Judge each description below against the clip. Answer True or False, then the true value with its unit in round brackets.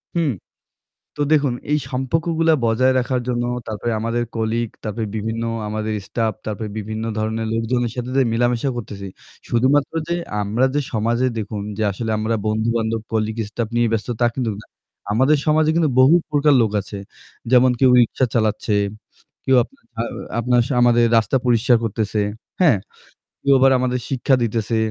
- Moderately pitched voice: False (120 Hz)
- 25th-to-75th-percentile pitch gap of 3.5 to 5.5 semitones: False (2.9 semitones)